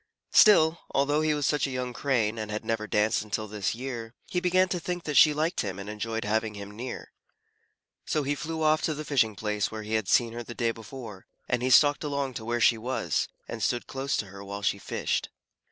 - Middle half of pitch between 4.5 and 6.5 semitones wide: Yes, average, 5.2 semitones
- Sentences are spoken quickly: Yes, fast, 230 wpm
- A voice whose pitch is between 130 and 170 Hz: No, low, 120 Hz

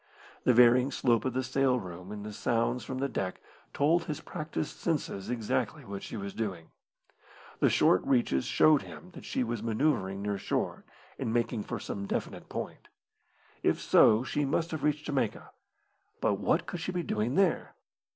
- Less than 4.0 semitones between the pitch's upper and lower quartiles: No, wide, 5.6 semitones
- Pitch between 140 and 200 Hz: No, low, 120 Hz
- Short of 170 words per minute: No, average, 175 wpm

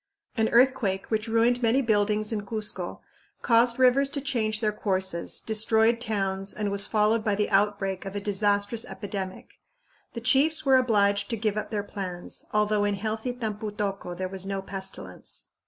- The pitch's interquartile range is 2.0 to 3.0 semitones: Yes, narrow, 2.4 semitones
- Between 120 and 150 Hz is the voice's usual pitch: No, high, 210 Hz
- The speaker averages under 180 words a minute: Yes, average, 170 wpm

